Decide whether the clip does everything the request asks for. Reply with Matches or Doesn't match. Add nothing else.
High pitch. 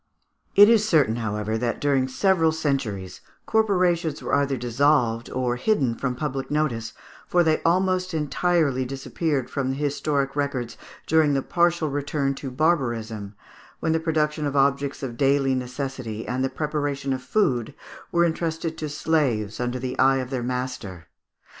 Doesn't match